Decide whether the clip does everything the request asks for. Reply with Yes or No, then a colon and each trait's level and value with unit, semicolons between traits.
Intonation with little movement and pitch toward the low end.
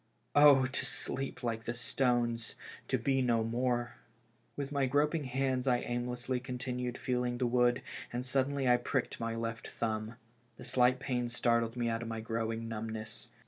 Yes: narrow, 2.0 semitones; low, 125 Hz